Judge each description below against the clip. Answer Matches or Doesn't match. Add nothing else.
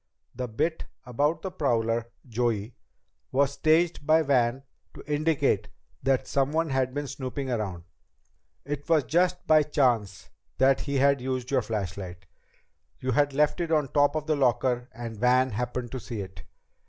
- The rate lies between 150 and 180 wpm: Matches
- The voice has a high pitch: Doesn't match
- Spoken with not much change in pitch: Doesn't match